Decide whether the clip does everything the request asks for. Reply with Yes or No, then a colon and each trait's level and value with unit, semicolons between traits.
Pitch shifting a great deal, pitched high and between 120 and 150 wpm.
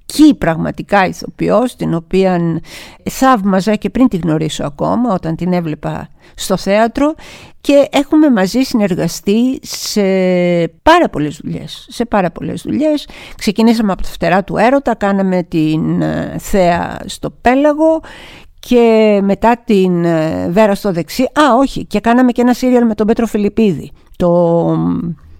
Yes: wide, 5.9 semitones; high, 205 Hz; average, 130 wpm